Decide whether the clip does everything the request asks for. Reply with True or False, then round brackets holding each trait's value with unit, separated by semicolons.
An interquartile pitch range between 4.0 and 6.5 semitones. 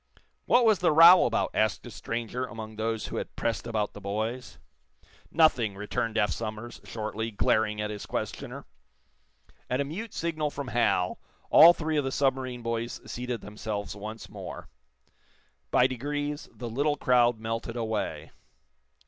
True (4.3 semitones)